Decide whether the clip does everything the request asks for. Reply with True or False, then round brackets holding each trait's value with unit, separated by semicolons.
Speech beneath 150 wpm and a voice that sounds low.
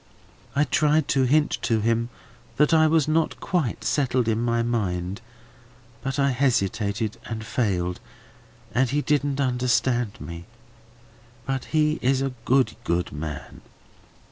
True (135 wpm; 125 Hz)